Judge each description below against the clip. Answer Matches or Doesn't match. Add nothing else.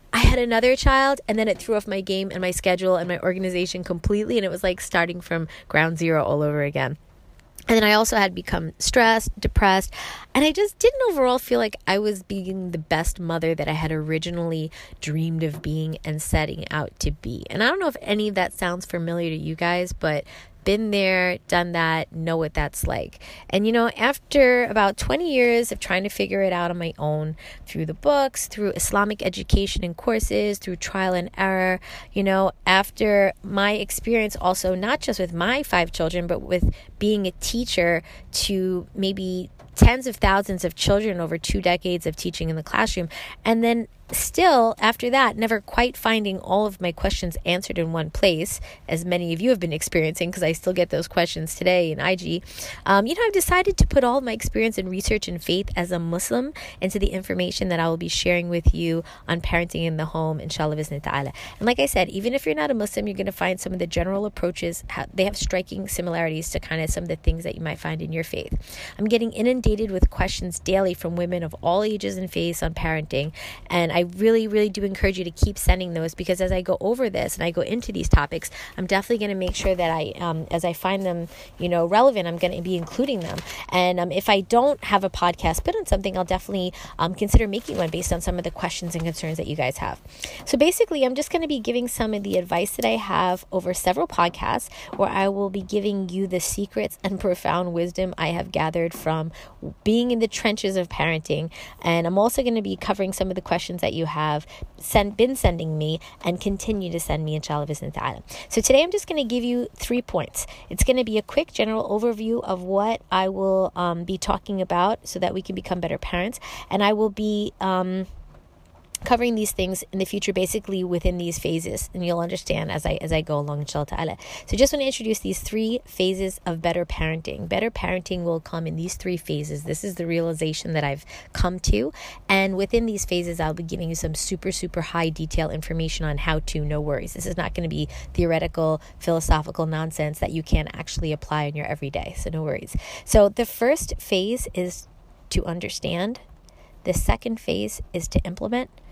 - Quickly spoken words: Matches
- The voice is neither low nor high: Matches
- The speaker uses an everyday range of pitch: Matches